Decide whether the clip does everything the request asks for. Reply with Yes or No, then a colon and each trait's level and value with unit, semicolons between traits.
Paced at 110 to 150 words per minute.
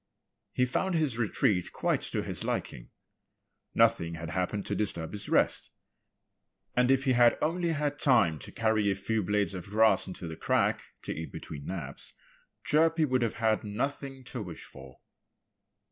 No: average, 165 wpm